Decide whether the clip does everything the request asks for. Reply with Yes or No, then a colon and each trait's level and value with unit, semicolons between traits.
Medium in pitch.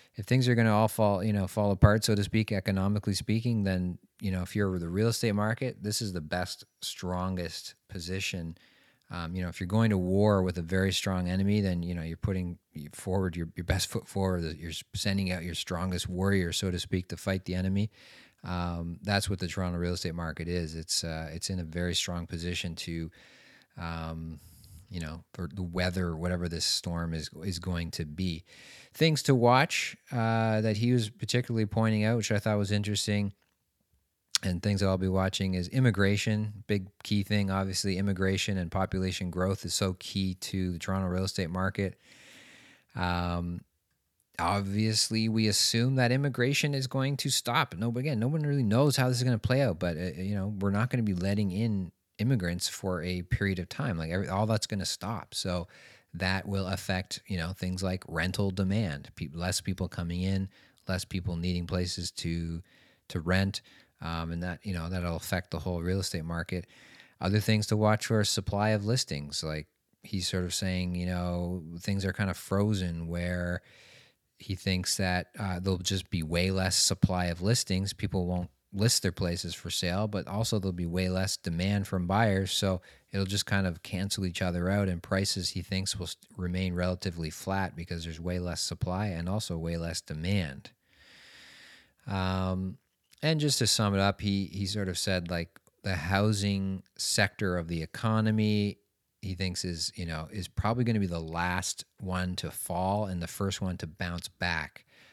No: very low, 95 Hz